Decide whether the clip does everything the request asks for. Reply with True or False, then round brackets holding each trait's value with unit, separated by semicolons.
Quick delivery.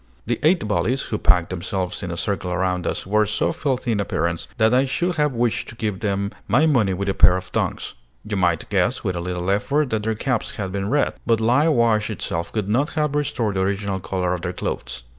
True (230 wpm)